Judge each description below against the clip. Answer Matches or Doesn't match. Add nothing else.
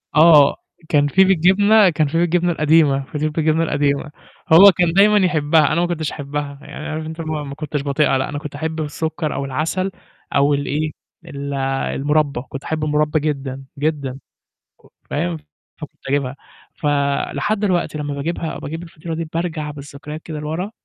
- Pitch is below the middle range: Doesn't match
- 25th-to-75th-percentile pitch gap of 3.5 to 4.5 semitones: Doesn't match